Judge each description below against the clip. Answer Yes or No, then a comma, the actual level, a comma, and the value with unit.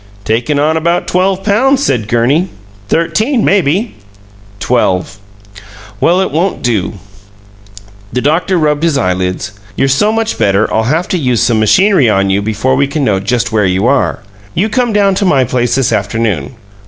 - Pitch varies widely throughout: Yes, wide, 8.7 semitones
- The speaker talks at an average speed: Yes, average, 165 wpm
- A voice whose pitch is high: No, low, 135 Hz